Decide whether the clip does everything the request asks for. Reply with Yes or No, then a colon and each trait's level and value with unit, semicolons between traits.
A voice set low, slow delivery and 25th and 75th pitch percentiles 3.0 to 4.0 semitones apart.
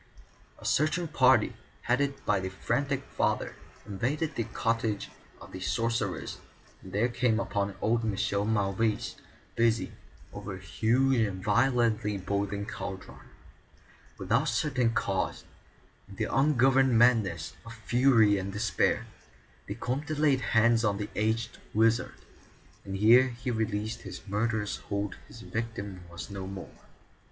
Yes: low, 110 Hz; slow, 130 wpm; average, 3.4 semitones